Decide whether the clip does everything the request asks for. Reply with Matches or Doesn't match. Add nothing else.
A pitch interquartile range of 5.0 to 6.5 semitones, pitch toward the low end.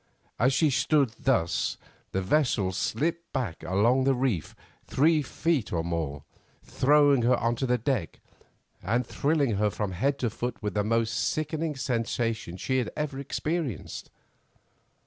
Matches